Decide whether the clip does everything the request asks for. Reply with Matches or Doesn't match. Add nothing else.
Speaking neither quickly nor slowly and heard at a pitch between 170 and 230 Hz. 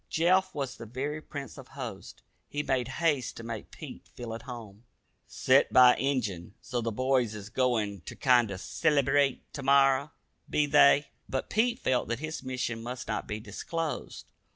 Doesn't match